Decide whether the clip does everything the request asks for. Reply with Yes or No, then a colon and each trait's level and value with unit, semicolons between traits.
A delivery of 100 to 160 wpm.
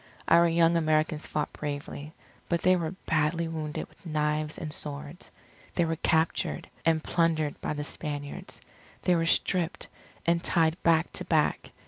Yes: average, 150 wpm